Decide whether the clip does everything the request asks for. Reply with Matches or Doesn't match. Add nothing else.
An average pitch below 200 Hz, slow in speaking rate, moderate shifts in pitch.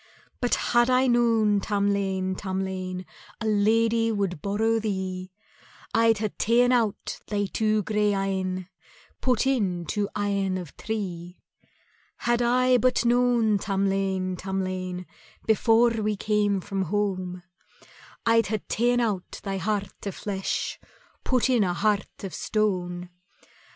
Doesn't match